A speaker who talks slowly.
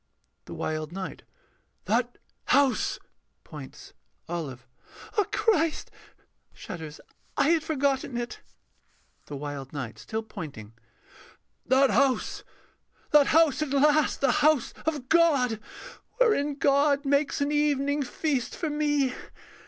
Yes: slow, 115 wpm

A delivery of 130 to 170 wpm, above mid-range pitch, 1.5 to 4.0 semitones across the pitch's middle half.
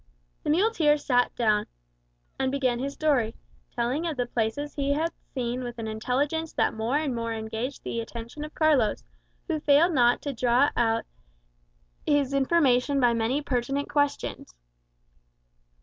Yes: average, 150 wpm; very high, 260 Hz; average, 3.7 semitones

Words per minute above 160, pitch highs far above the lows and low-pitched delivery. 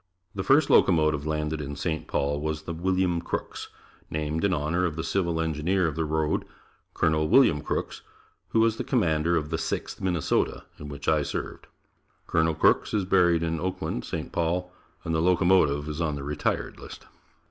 No: average, 180 wpm; average, 2.8 semitones; very low, 80 Hz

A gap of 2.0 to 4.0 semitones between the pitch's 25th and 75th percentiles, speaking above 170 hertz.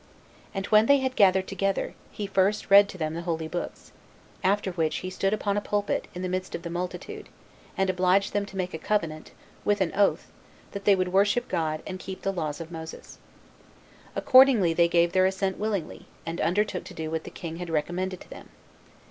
Yes: average, 3.0 semitones; medium, 185 Hz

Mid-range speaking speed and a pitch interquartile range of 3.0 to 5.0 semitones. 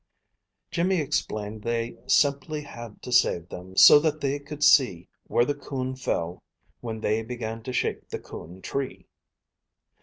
Yes: average, 150 wpm; average, 4.7 semitones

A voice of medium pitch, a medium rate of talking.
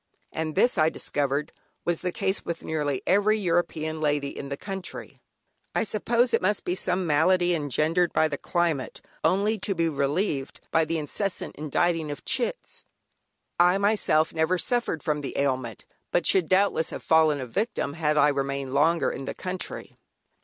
Yes: medium, 160 Hz; average, 165 wpm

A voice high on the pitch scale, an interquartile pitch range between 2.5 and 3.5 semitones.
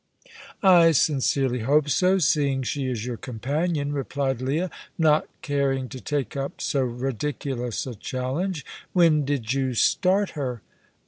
No: medium, 140 Hz; average, 2.9 semitones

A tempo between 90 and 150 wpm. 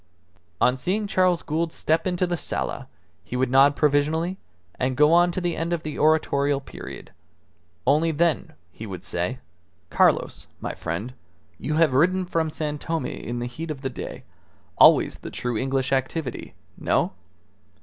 No: average, 160 wpm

